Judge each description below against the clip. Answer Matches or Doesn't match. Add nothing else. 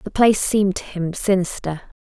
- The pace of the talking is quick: Doesn't match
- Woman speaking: Matches